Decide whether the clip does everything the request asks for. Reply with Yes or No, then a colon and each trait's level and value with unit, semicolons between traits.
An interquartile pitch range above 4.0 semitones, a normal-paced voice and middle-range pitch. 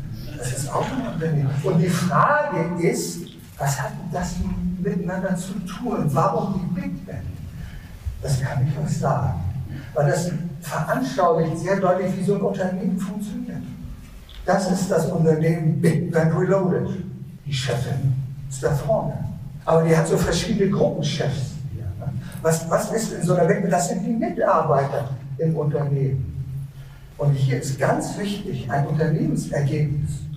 Yes: average, 4.7 semitones; average, 140 wpm; medium, 160 Hz